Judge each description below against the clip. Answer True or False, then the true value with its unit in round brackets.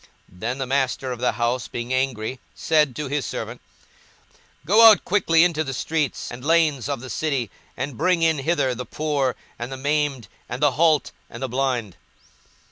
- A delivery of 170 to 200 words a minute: True (180 wpm)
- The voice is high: False (135 Hz)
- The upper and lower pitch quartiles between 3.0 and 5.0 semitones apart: True (3.7 semitones)